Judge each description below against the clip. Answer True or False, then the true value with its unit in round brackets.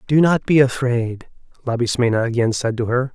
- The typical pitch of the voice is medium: False (125 Hz)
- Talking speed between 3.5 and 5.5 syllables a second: True (5.3 syllables/s)